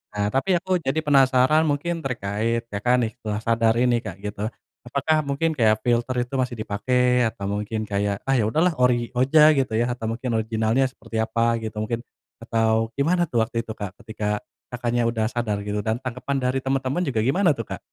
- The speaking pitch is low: Yes, low, 120 Hz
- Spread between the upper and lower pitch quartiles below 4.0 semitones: Yes, average, 3.4 semitones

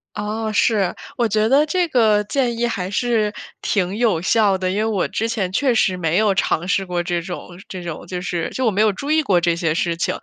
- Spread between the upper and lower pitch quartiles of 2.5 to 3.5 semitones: No, average, 4.1 semitones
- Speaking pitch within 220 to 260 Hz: No, high, 205 Hz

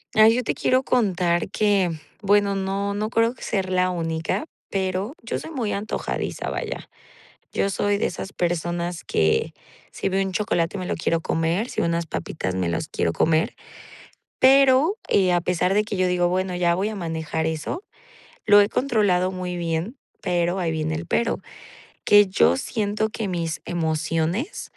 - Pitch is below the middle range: No, medium, 185 Hz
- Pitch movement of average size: Yes, average, 3.7 semitones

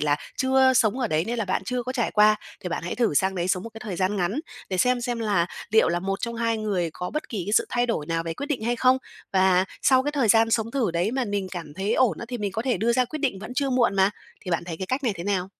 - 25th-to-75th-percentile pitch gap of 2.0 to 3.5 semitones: No, average, 4.8 semitones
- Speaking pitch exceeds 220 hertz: No, high, 215 Hz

